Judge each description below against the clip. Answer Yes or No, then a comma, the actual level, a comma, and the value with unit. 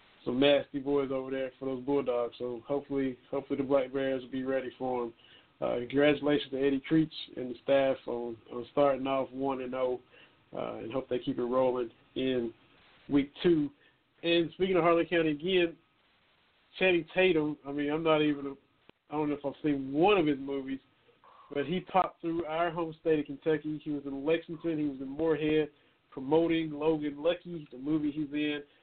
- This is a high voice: No, medium, 140 Hz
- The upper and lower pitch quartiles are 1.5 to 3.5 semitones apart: Yes, average, 2.9 semitones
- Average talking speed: Yes, average, 190 wpm